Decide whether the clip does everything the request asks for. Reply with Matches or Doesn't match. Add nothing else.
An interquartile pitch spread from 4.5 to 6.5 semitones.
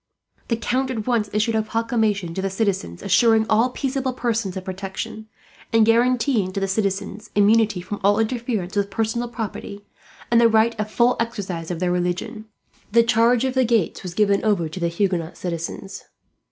Doesn't match